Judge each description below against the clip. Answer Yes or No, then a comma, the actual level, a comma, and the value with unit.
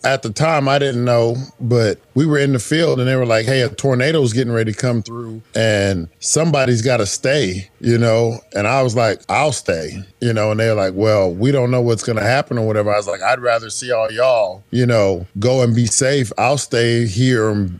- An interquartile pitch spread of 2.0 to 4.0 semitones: Yes, average, 3.0 semitones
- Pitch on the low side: Yes, low, 115 Hz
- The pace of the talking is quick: Yes, fast, 240 wpm